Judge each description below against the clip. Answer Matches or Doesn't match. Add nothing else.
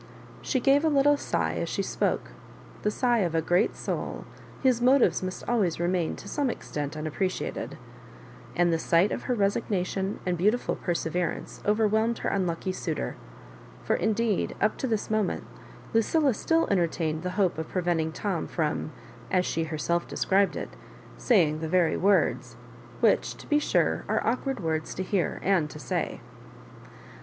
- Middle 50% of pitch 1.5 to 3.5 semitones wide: Doesn't match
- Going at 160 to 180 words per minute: Matches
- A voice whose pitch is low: Doesn't match